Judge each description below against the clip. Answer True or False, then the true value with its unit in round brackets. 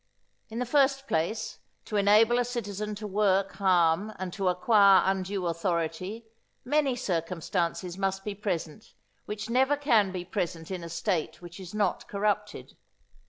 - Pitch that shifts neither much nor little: True (3.3 semitones)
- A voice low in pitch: False (200 Hz)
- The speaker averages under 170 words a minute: True (150 wpm)